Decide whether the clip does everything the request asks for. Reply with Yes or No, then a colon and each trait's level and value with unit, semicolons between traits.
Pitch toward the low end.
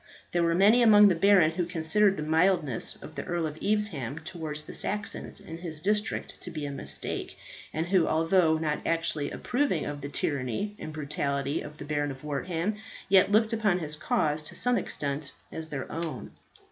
No: medium, 165 Hz